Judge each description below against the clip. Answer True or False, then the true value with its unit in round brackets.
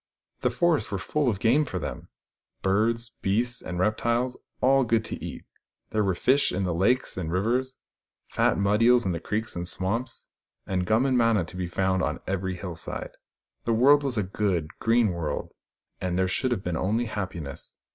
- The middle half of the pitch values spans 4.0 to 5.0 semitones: True (4.6 semitones)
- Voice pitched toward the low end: True (105 Hz)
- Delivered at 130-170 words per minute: False (195 wpm)